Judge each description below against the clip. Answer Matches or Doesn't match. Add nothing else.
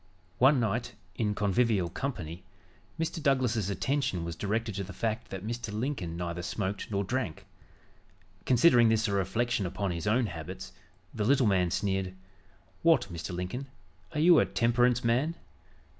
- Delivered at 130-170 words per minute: Matches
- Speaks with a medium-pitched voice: Doesn't match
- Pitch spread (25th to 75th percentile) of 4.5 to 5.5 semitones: Matches